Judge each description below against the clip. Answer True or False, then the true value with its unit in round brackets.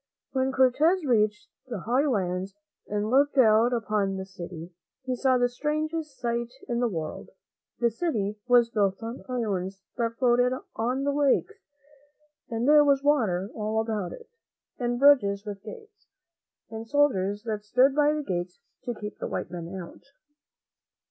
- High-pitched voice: True (235 Hz)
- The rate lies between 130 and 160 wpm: True (155 wpm)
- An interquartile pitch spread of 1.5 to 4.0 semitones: False (4.6 semitones)